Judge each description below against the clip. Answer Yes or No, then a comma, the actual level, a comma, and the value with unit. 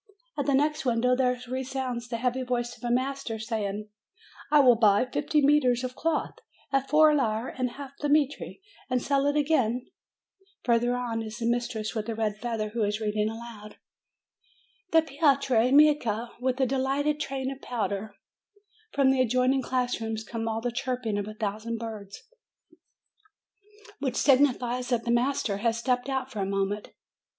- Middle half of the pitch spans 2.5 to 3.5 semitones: Yes, average, 3.2 semitones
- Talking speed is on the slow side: No, average, 175 wpm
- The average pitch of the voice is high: Yes, high, 245 Hz